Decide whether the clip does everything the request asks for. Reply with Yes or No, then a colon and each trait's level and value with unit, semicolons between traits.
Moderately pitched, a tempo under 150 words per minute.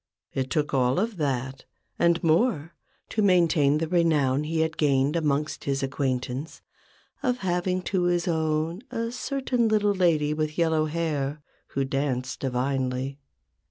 Yes: medium, 155 Hz; average, 140 wpm